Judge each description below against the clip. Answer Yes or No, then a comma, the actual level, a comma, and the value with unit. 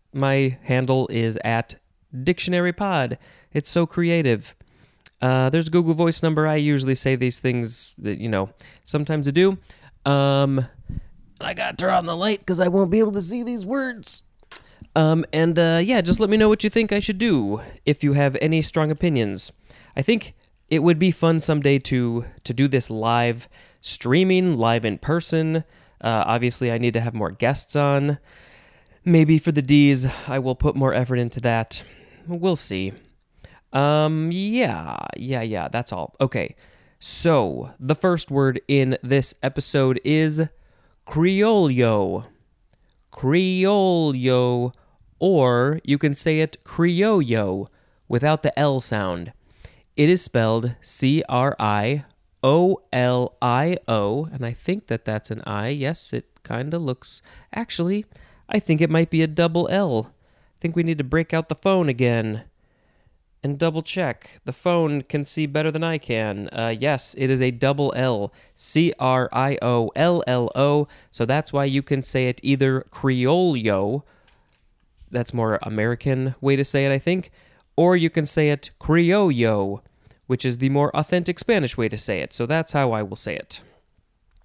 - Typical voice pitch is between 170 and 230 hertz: No, medium, 140 Hz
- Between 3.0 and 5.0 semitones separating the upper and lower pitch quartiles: No, wide, 5.5 semitones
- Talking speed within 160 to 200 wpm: Yes, average, 165 wpm